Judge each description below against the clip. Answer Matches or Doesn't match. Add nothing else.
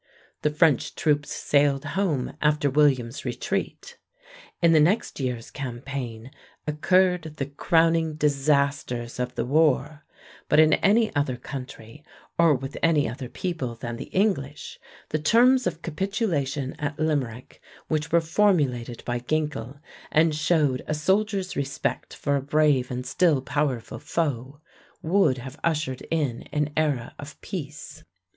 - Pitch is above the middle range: Doesn't match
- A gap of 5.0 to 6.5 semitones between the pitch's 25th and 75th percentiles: Doesn't match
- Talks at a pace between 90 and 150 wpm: Matches